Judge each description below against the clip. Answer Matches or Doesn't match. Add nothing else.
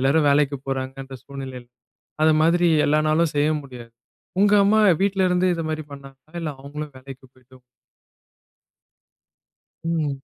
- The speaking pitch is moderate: Matches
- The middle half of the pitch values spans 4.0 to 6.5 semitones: Doesn't match